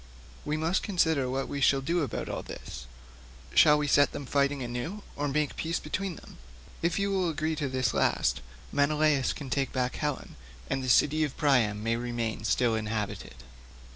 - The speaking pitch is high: No, medium, 140 Hz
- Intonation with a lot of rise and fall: No, average, 4.0 semitones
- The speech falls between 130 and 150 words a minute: No, average, 180 wpm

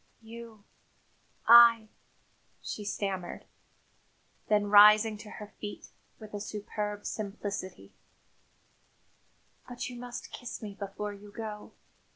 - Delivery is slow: Yes, slow, 110 wpm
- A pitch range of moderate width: No, narrow, 1.5 semitones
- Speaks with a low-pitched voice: No, high, 210 Hz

